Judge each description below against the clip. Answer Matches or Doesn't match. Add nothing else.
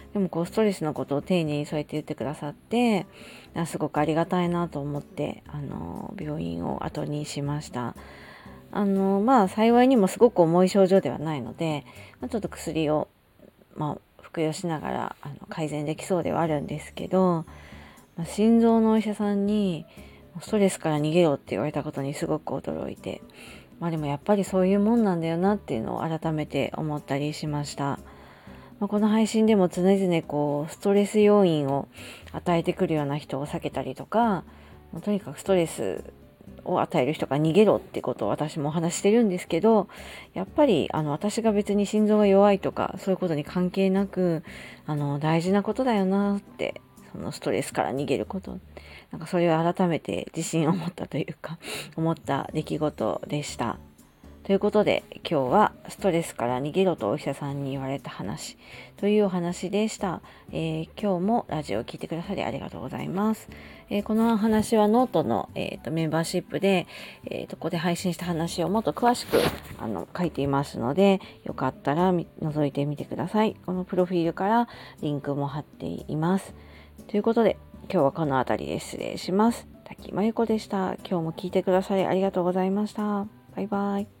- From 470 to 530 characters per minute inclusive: Doesn't match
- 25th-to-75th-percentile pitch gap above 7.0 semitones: Doesn't match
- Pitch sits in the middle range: Matches